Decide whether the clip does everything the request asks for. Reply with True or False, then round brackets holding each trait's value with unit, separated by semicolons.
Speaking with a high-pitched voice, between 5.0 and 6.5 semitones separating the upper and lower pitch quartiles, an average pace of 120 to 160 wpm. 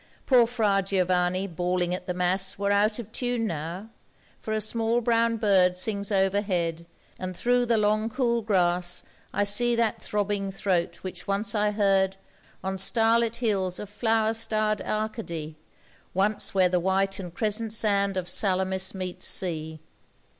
False (200 Hz; 3.1 semitones; 155 wpm)